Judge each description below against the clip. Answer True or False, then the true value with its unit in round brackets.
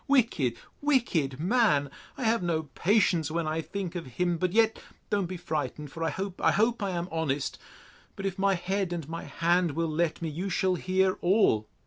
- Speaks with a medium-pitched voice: True (175 Hz)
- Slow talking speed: False (165 wpm)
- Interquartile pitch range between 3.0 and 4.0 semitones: True (3.6 semitones)